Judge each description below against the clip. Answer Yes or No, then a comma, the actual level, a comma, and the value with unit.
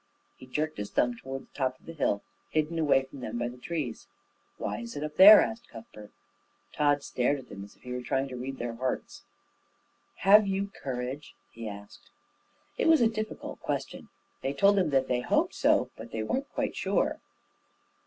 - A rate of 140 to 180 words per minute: No, average, 200 wpm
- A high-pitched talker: No, low, 135 Hz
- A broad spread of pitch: No, average, 4.4 semitones